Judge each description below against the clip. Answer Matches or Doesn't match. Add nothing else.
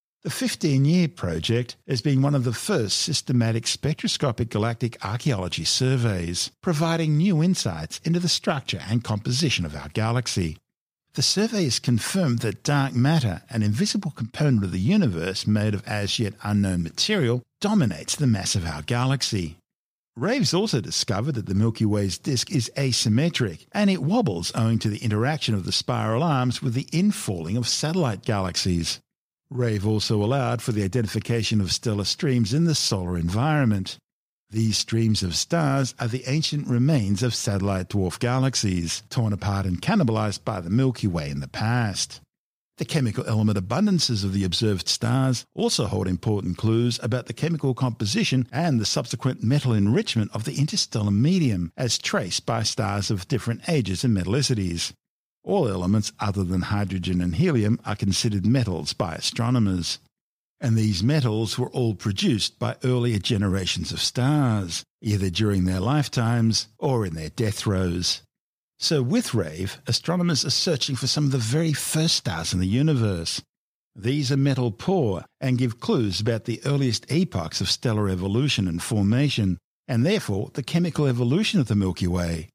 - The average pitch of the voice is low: Matches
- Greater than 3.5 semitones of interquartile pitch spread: Matches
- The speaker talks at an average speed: Matches